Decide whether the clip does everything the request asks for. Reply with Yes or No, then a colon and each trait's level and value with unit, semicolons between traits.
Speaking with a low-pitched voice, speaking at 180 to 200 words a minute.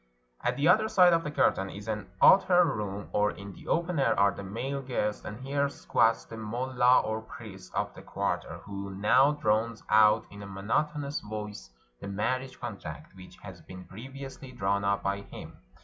Yes: low, 110 Hz; average, 185 wpm